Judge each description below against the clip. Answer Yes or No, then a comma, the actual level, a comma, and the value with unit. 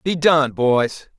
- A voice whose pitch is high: No, medium, 145 Hz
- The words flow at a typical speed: Yes, average, 150 wpm